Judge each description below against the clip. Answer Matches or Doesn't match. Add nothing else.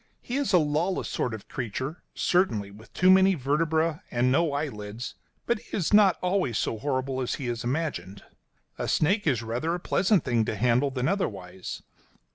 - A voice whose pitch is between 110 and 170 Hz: Matches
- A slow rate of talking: Doesn't match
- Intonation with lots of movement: Matches